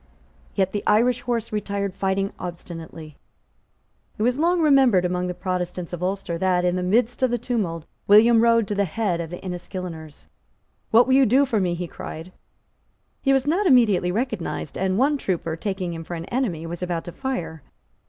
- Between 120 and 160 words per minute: No, average, 185 wpm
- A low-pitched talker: No, high, 190 Hz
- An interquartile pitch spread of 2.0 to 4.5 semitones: No, average, 5.2 semitones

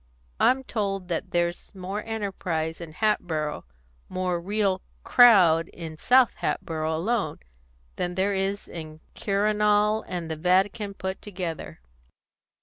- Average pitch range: Yes, average, 3.8 semitones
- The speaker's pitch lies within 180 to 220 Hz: Yes, high, 190 Hz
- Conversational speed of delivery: No, slow, 125 wpm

